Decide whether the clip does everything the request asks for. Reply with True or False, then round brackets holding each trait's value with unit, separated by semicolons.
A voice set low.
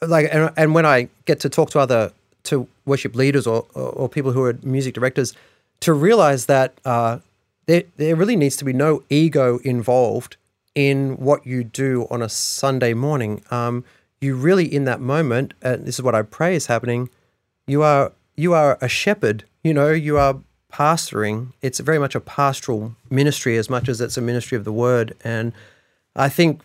True (130 Hz)